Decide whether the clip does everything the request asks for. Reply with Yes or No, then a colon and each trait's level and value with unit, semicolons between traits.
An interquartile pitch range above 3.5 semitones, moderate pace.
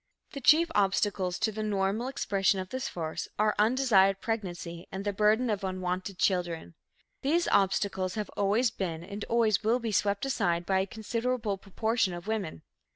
No: average, 3.0 semitones; average, 165 wpm